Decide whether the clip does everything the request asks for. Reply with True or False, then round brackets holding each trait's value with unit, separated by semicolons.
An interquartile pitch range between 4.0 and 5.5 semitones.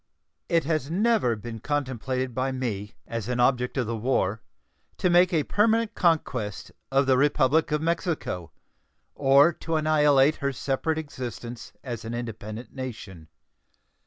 True (4.8 semitones)